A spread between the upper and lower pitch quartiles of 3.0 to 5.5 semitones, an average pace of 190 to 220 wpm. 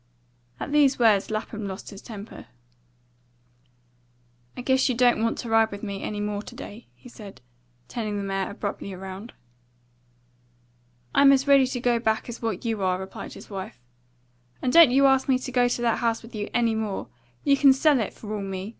Yes: average, 3.8 semitones; average, 195 wpm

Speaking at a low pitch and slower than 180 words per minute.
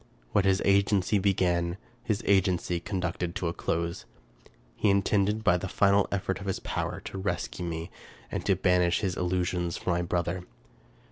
Yes: very low, 90 Hz; average, 160 wpm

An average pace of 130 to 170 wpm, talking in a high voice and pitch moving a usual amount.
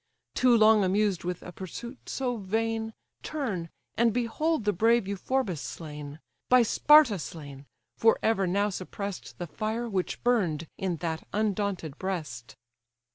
Yes: slow, 135 wpm; high, 205 Hz; average, 4.6 semitones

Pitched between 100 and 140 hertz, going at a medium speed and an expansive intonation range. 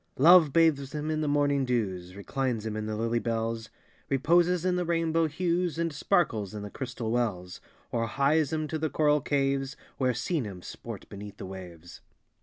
Yes: low, 135 Hz; average, 185 wpm; wide, 6.1 semitones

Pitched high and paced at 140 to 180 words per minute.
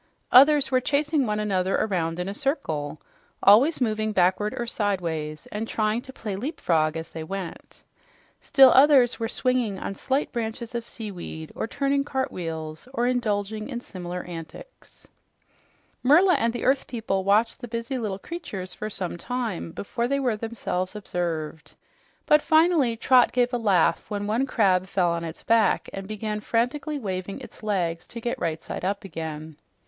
Yes: high, 215 Hz; average, 165 wpm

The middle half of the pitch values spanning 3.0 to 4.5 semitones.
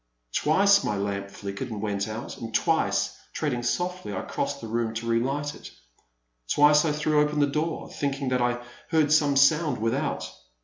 No: average, 5.0 semitones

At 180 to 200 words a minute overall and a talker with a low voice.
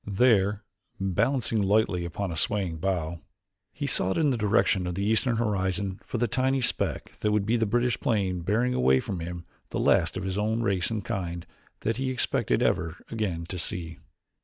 Yes: average, 185 wpm; low, 100 Hz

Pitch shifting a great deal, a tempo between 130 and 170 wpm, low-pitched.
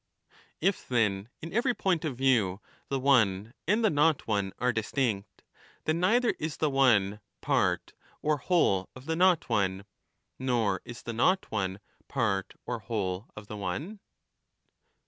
Yes: wide, 7.5 semitones; average, 160 wpm; low, 125 Hz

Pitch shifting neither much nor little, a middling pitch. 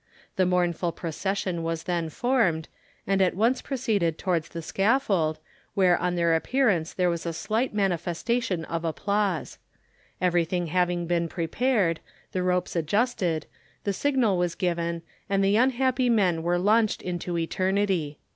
Yes: average, 3.4 semitones; medium, 180 Hz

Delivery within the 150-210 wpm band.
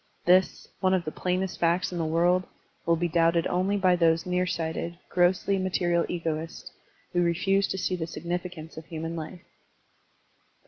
Yes: average, 165 wpm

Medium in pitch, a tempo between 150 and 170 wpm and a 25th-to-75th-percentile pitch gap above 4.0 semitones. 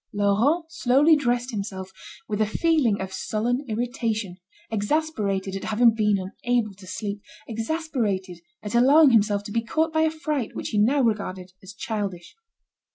No: high, 220 Hz; average, 155 wpm; average, 4.7 semitones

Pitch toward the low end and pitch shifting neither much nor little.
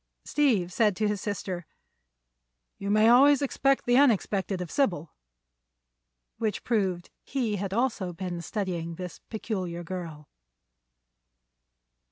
No: high, 200 Hz; average, 4.5 semitones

